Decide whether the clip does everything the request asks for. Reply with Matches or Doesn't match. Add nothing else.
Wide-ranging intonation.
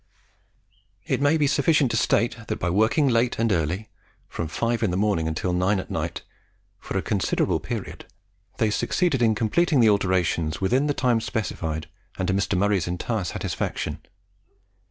Doesn't match